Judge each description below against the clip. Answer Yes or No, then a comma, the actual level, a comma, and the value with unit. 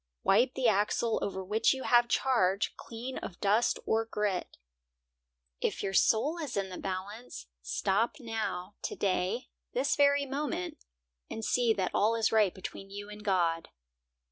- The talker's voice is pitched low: No, high, 210 Hz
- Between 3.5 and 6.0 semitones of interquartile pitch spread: Yes, average, 3.8 semitones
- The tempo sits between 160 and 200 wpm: No, average, 150 wpm